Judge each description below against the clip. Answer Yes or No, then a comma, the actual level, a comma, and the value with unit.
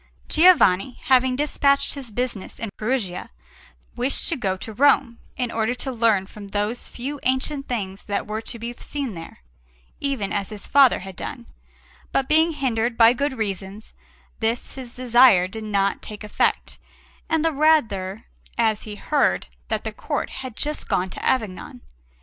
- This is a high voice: Yes, high, 235 Hz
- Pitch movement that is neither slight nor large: Yes, average, 4.6 semitones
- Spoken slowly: No, average, 160 wpm